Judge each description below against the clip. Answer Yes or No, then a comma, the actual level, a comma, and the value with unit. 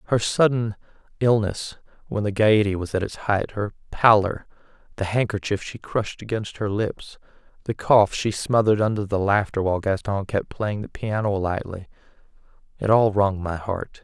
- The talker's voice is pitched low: Yes, low, 105 Hz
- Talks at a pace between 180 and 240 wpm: No, average, 160 wpm